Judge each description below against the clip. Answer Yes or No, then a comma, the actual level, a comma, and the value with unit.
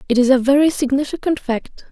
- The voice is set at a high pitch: Yes, very high, 265 Hz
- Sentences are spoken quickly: No, average, 190 wpm